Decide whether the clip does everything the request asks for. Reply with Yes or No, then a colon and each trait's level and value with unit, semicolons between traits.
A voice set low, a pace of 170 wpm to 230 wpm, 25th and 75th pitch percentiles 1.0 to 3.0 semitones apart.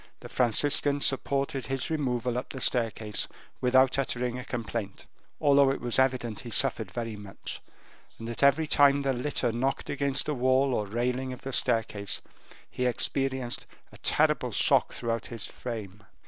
No: low, 125 Hz; average, 160 wpm; average, 2.7 semitones